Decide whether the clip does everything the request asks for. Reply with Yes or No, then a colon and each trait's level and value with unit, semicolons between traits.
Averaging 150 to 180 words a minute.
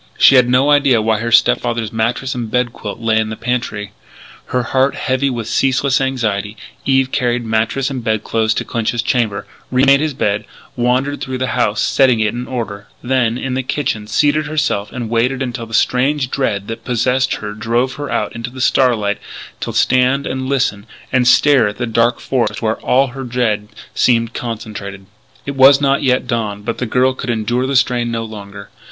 No: average, 195 wpm